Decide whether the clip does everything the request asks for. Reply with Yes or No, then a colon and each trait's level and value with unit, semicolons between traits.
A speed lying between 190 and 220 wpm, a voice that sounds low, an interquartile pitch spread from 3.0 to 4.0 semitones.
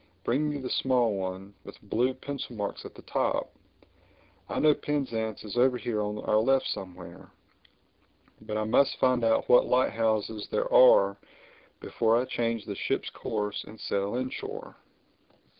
No: average, 155 wpm; low, 115 Hz; average, 3.7 semitones